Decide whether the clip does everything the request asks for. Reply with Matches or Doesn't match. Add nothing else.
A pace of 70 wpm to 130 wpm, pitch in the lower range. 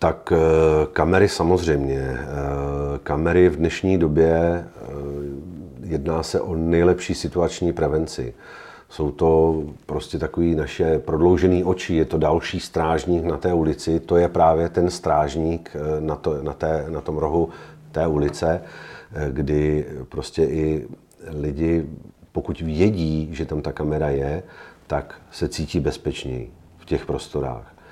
Matches